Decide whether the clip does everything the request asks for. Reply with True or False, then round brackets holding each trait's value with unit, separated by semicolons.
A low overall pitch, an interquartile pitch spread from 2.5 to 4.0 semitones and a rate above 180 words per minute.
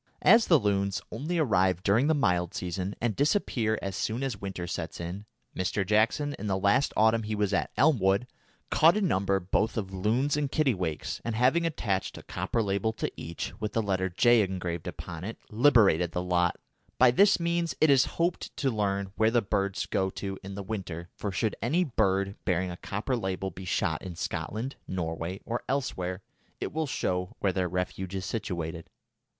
False (100 Hz; 4.6 semitones; 190 wpm)